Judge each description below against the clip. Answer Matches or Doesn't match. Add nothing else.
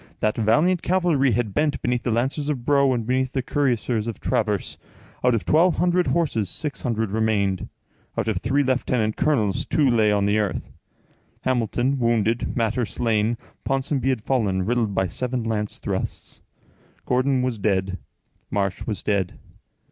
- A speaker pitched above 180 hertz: Doesn't match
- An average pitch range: Matches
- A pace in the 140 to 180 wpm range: Matches